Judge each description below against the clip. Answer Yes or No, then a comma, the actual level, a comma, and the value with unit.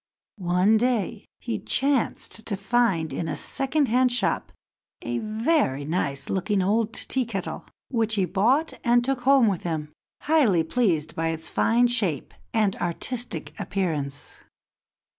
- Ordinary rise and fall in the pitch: No, wide, 5.8 semitones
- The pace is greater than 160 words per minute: No, average, 140 wpm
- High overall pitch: Yes, high, 215 Hz